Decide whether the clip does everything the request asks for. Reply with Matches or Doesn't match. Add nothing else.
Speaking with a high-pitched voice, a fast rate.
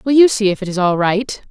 Matches